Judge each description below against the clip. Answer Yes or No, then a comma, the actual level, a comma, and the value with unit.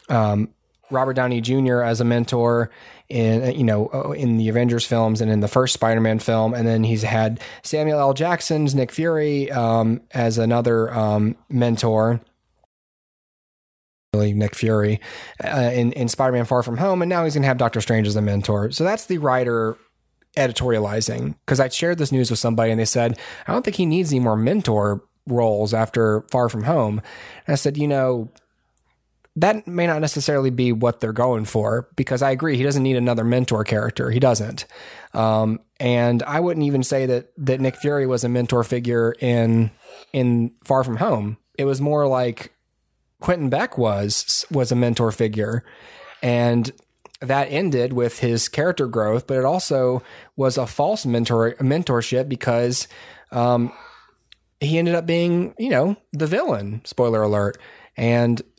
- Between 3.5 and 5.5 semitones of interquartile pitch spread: No, average, 3.1 semitones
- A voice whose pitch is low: Yes, low, 120 Hz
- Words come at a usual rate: Yes, average, 170 wpm